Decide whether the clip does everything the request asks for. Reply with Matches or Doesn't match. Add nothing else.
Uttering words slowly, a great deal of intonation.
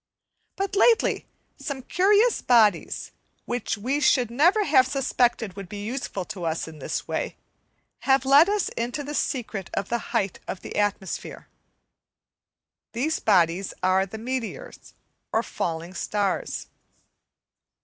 Matches